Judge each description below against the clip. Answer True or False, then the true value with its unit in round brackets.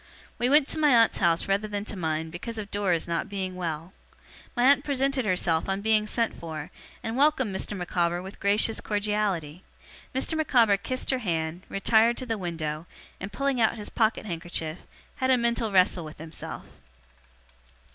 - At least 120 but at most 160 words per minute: False (175 wpm)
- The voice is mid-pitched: False (205 Hz)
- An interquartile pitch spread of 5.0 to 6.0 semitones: True (5.3 semitones)